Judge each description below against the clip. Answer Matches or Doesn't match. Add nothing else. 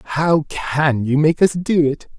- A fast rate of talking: Doesn't match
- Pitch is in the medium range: Matches